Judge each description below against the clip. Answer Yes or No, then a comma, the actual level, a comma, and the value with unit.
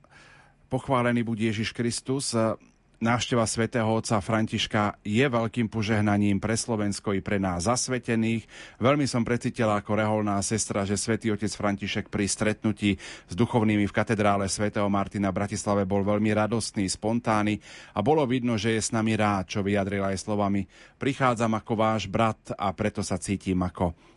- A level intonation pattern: Yes, narrow, 2.2 semitones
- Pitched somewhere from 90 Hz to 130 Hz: Yes, low, 110 Hz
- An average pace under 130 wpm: No, average, 155 wpm